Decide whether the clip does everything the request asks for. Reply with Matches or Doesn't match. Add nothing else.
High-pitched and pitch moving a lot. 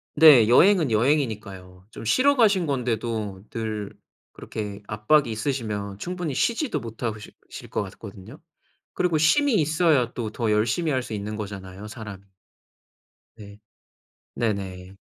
Doesn't match